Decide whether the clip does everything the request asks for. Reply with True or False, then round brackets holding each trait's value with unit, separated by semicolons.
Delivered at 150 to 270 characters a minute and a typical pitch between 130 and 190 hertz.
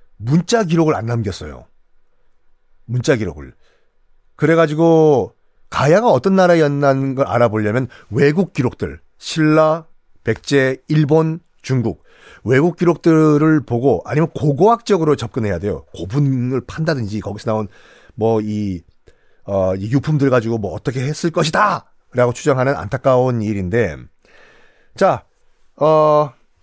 True (265 characters per minute; 135 Hz)